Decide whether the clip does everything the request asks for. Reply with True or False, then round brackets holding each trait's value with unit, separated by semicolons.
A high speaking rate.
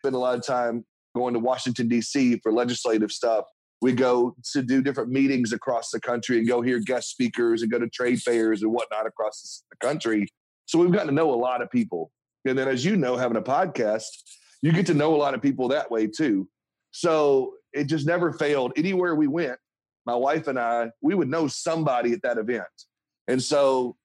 True (210 wpm)